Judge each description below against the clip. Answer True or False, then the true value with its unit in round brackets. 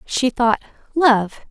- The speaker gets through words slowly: True (120 wpm)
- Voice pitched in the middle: False (250 Hz)